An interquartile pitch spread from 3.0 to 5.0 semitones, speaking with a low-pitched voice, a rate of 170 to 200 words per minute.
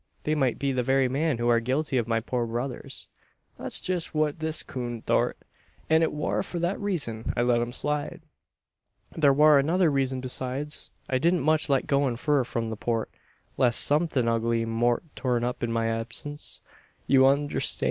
Yes: average, 4.0 semitones; low, 130 Hz; average, 185 wpm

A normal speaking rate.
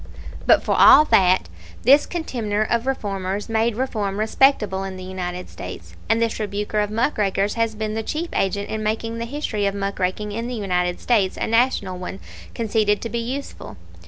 Yes: average, 190 wpm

